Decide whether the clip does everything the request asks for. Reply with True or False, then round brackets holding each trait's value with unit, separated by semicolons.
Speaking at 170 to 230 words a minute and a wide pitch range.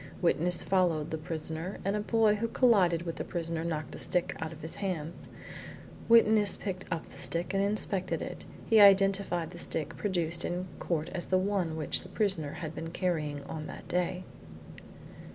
False (180 wpm; 3.3 semitones)